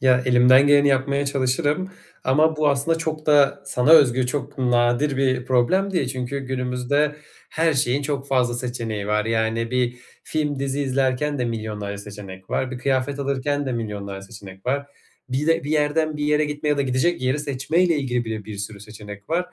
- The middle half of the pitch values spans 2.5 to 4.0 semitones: Yes, average, 3.3 semitones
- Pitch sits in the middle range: No, low, 130 Hz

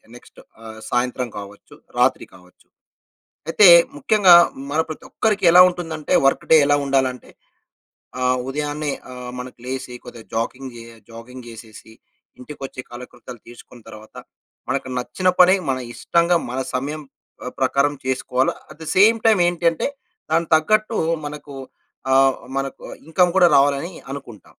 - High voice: No, low, 135 Hz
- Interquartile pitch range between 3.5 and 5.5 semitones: Yes, average, 4.6 semitones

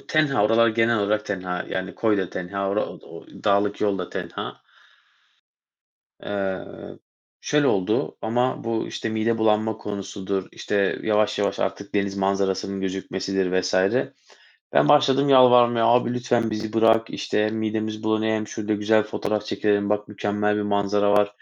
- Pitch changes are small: Yes, narrow, 2.0 semitones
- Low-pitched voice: Yes, low, 105 Hz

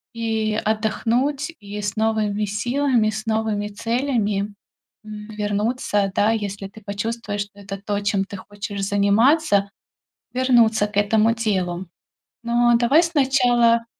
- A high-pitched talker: Yes, high, 215 Hz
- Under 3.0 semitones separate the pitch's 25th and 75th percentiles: Yes, narrow, 2.5 semitones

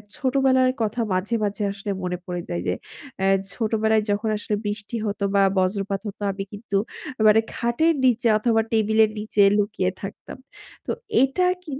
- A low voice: No, high, 215 Hz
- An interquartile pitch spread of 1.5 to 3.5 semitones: Yes, average, 2.9 semitones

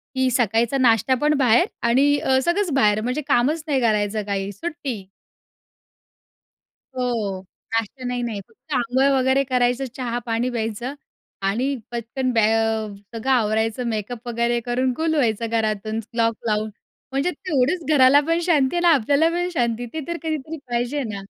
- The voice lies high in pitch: Yes, high, 245 Hz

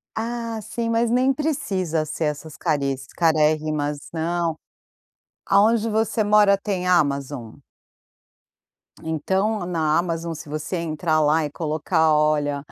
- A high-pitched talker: No, medium, 165 Hz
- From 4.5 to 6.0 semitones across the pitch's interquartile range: Yes, average, 5.3 semitones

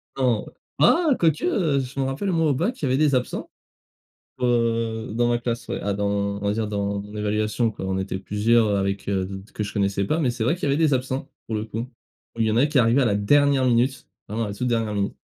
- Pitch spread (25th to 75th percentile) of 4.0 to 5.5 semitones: Yes, average, 4.5 semitones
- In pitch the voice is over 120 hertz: No, low, 115 Hz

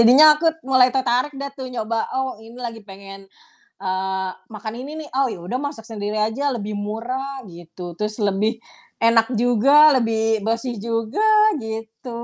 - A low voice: No, high, 230 Hz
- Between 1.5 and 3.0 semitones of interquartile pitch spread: No, average, 3.4 semitones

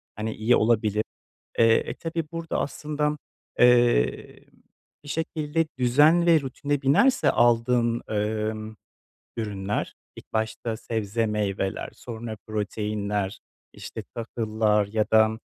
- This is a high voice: No, low, 115 Hz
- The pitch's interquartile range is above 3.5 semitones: Yes, average, 4.0 semitones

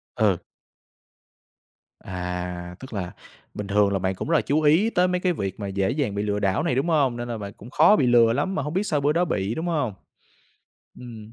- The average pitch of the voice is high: No, low, 120 Hz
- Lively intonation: Yes, wide, 7.2 semitones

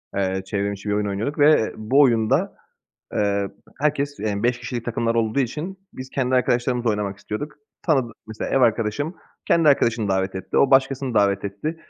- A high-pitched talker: No, low, 115 Hz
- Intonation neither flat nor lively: Yes, average, 4.9 semitones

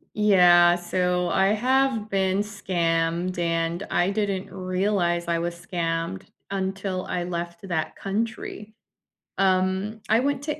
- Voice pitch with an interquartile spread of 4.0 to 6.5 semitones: No, average, 3.0 semitones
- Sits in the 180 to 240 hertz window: Yes, medium, 185 Hz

